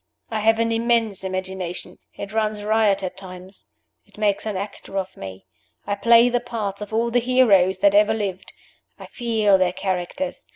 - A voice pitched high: Yes, high, 210 Hz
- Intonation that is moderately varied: Yes, average, 3.3 semitones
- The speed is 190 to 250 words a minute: No, average, 175 wpm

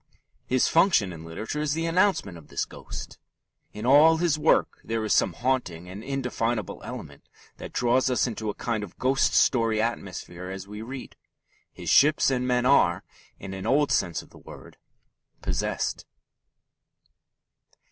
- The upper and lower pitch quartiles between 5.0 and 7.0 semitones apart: Yes, wide, 5.5 semitones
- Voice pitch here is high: No, low, 120 Hz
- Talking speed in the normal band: Yes, average, 155 wpm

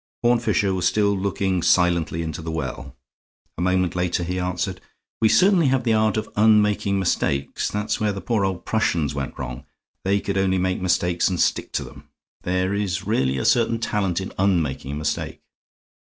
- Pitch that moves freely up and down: No, average, 3.4 semitones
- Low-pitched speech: Yes, very low, 95 Hz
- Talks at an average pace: Yes, average, 180 wpm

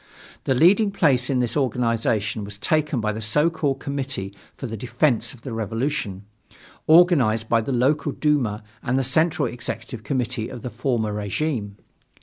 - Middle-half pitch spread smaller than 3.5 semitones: No, average, 4.6 semitones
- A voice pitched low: Yes, low, 125 Hz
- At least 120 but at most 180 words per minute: Yes, average, 160 wpm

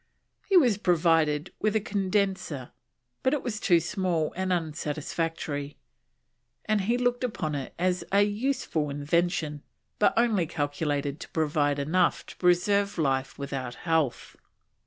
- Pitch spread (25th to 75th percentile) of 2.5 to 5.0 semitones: No, wide, 5.5 semitones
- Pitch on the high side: No, medium, 170 Hz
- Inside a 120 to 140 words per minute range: Yes, slow, 135 wpm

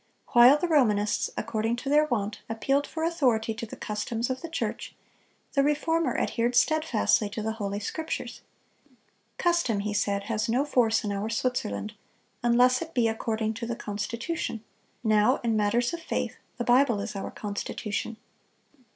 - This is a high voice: Yes, high, 230 Hz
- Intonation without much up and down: No, average, 4.2 semitones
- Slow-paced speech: No, average, 160 wpm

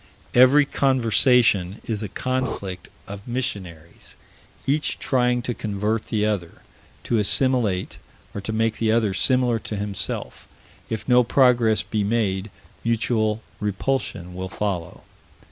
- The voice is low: Yes, low, 110 Hz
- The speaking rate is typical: No, slow, 125 wpm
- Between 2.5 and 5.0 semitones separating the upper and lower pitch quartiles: Yes, average, 3.6 semitones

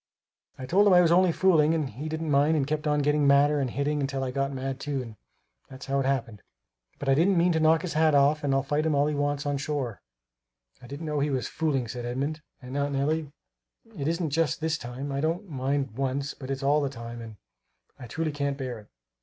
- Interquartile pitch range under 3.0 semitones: Yes, narrow, 2.4 semitones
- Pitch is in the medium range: Yes, medium, 145 Hz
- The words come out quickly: Yes, fast, 245 wpm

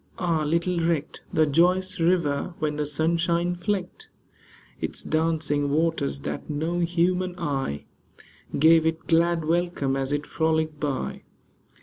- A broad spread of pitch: No, average, 2.7 semitones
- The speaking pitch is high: No, medium, 160 Hz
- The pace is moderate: No, slow, 125 wpm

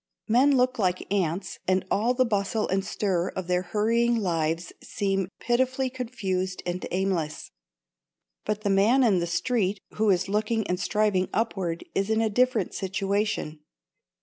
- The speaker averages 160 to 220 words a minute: No, average, 150 wpm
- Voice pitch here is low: No, high, 200 Hz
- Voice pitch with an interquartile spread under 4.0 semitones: Yes, average, 3.6 semitones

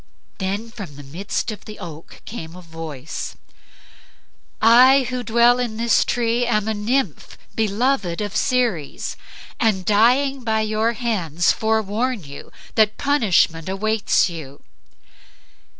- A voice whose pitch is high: Yes, high, 215 Hz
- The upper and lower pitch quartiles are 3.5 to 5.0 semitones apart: Yes, average, 4.7 semitones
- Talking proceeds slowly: Yes, slow, 125 wpm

